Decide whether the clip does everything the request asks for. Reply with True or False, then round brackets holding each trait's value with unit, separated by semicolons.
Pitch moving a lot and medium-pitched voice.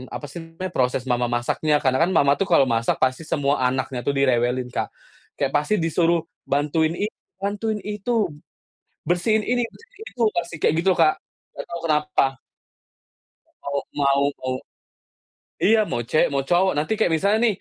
True (5.9 semitones; 155 Hz)